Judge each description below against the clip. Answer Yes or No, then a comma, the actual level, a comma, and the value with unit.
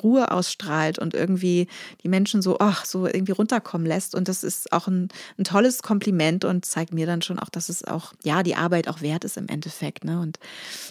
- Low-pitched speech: No, medium, 180 Hz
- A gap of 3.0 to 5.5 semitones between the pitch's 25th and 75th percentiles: No, narrow, 2.6 semitones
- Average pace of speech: No, fast, 215 wpm